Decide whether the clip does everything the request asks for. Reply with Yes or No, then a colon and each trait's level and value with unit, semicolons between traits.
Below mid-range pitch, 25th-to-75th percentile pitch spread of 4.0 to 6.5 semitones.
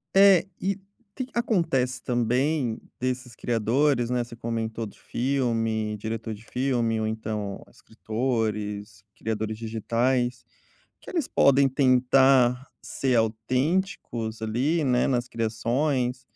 No: low, 120 Hz; average, 3.1 semitones